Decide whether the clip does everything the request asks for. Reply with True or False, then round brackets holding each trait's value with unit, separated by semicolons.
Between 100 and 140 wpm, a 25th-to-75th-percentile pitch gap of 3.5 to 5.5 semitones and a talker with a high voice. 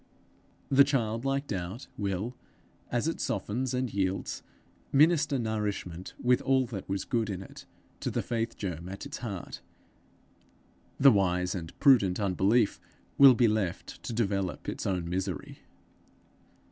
False (135 wpm; 4.9 semitones; 105 Hz)